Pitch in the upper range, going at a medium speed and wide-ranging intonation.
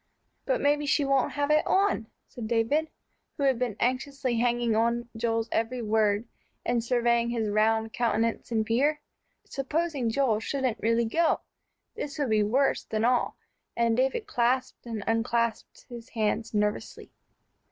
No: high, 235 Hz; average, 150 wpm; average, 3.2 semitones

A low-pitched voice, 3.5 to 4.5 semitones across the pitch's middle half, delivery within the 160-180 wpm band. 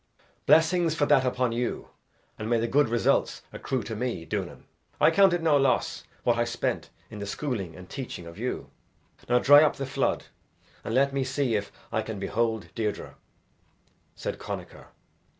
Yes: low, 125 Hz; average, 4.0 semitones; average, 175 wpm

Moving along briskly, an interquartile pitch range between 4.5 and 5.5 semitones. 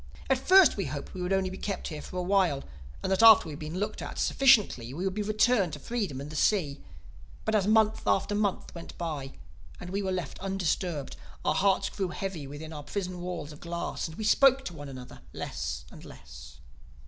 Yes: fast, 220 wpm; average, 5.2 semitones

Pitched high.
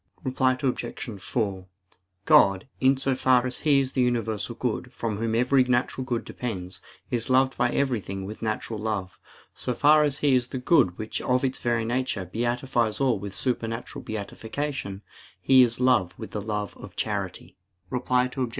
No: low, 120 Hz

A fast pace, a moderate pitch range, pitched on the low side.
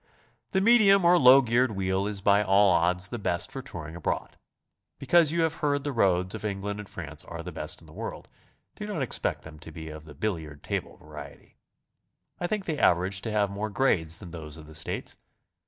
No: fast, 210 wpm; wide, 7.8 semitones; low, 100 Hz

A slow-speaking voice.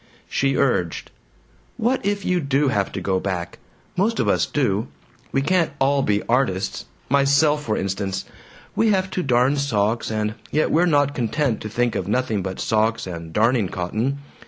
No: average, 170 wpm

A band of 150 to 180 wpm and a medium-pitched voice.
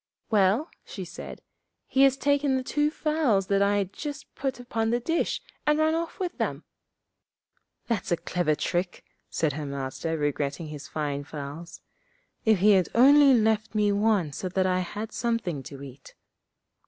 No: average, 165 wpm; high, 205 Hz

